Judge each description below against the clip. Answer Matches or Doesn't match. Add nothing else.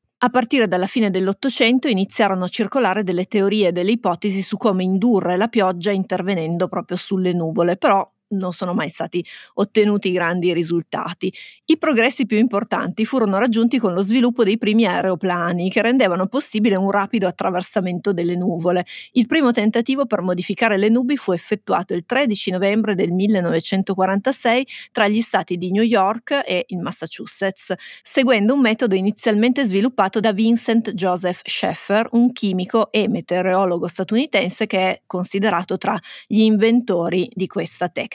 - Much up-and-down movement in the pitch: Doesn't match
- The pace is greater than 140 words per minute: Matches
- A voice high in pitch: Matches